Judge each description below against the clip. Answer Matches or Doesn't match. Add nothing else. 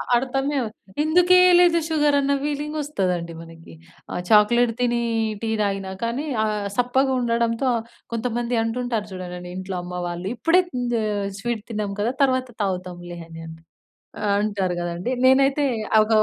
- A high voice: Matches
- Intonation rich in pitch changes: Matches